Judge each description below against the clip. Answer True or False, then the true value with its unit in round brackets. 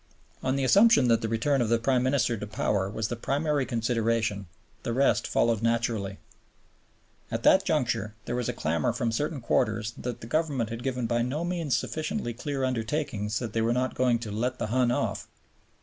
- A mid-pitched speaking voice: False (120 Hz)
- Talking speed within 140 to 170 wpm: False (195 wpm)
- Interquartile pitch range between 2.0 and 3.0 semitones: True (2.7 semitones)